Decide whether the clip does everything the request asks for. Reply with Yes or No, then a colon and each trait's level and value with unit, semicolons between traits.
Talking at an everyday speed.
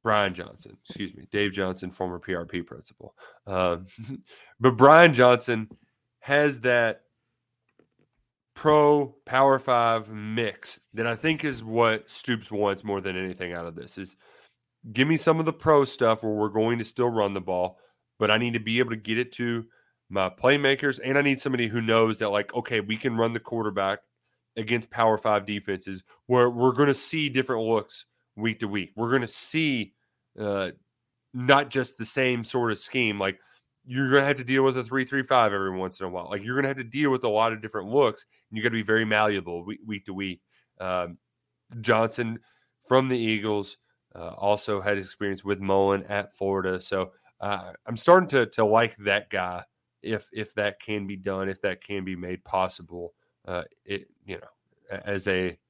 Yes: average, 190 wpm